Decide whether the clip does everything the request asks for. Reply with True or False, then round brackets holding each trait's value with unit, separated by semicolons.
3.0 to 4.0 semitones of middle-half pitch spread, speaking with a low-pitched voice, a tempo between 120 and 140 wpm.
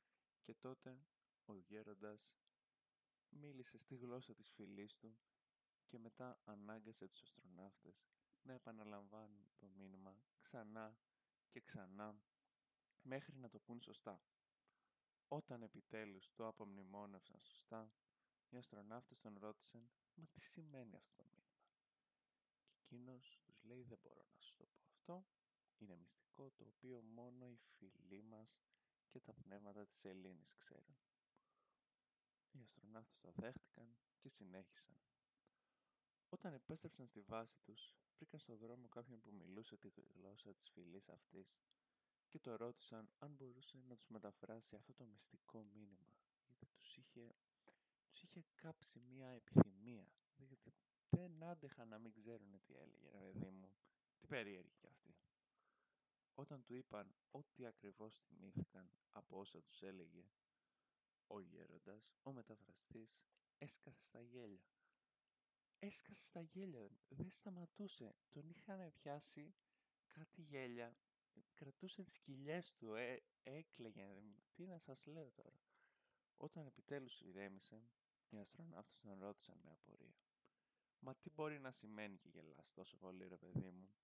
False (4.6 semitones; 120 Hz; 130 wpm)